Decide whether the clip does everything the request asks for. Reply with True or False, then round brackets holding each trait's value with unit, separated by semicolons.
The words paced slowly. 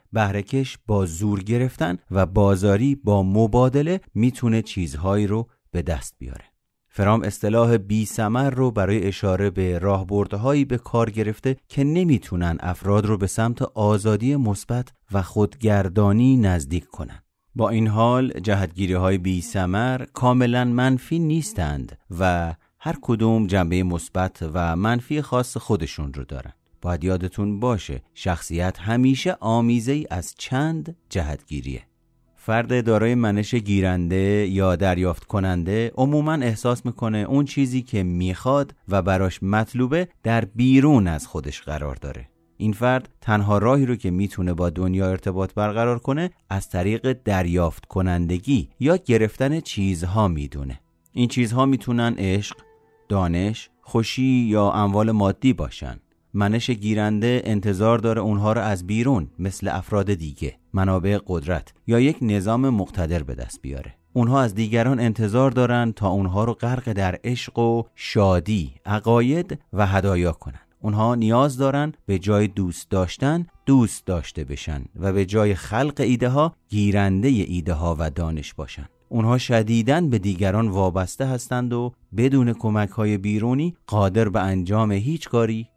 False (140 wpm)